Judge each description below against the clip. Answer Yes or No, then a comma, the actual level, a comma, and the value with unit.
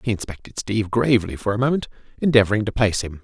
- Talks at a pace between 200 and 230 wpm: Yes, fast, 205 wpm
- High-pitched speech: No, low, 110 Hz